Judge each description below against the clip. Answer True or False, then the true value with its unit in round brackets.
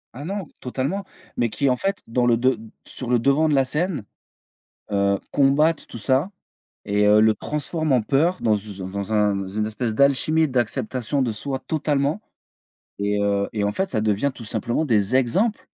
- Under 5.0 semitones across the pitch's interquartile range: False (5.5 semitones)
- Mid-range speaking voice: False (125 Hz)